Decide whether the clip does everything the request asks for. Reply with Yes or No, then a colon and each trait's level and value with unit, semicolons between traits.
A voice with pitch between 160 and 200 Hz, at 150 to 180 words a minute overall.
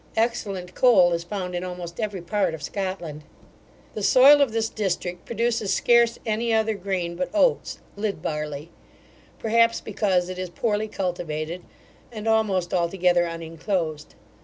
No: high, 190 Hz; average, 140 wpm